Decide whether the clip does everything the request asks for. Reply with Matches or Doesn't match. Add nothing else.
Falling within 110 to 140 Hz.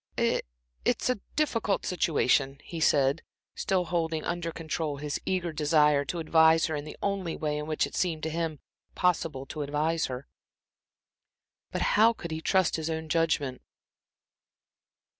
Doesn't match